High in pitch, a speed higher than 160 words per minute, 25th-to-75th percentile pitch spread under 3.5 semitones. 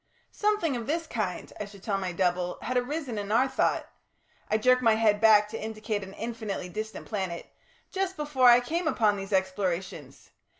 No: high, 220 Hz; average, 180 wpm; average, 4.4 semitones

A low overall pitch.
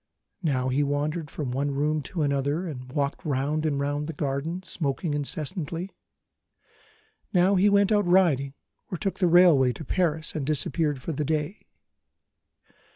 No: medium, 150 Hz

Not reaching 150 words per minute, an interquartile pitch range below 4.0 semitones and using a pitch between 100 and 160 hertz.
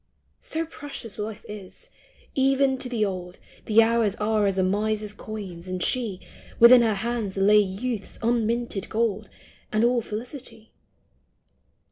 No: average, 140 wpm; average, 2.9 semitones; high, 220 Hz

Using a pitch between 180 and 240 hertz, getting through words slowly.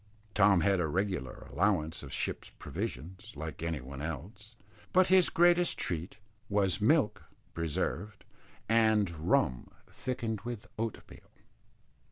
No: low, 100 Hz; slow, 120 wpm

